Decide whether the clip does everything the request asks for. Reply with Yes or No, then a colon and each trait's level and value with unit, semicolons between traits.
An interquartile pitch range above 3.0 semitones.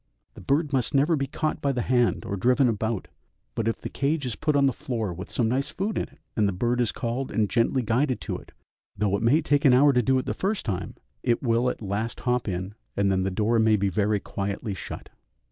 Yes: average, 4.6 semitones